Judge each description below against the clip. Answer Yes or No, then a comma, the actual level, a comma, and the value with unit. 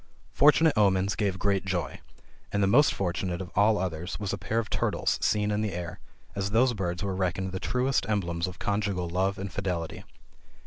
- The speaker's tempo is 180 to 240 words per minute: Yes, average, 190 wpm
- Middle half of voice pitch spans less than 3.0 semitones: Yes, narrow, 2.4 semitones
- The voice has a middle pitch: No, very low, 95 Hz